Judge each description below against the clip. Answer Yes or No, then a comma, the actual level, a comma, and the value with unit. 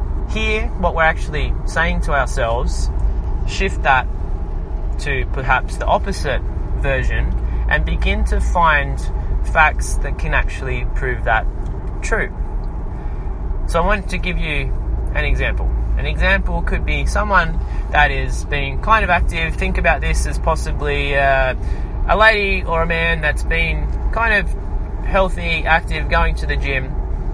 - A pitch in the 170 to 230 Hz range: No, very low, 80 Hz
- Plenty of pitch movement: Yes, wide, 8.1 semitones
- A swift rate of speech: No, average, 145 wpm